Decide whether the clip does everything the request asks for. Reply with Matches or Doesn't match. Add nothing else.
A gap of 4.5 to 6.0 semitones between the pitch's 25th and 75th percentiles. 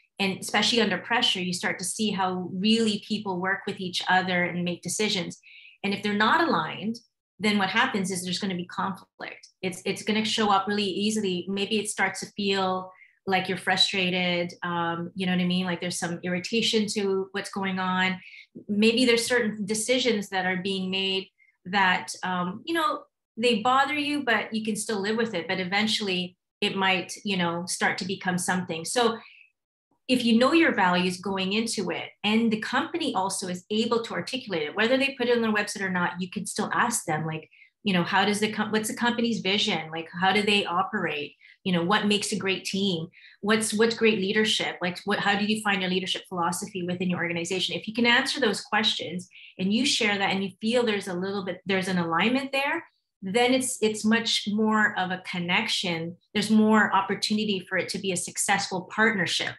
Doesn't match